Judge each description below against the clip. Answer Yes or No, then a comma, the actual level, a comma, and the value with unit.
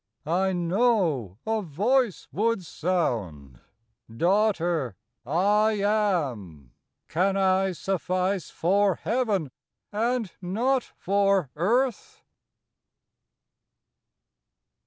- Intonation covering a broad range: No, average, 4.8 semitones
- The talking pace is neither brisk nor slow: No, slow, 75 wpm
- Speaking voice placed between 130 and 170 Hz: No, high, 190 Hz